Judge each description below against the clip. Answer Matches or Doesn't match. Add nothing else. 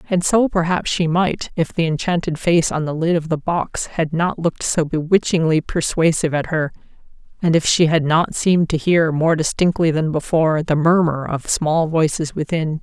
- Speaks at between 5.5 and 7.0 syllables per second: Doesn't match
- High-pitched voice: Doesn't match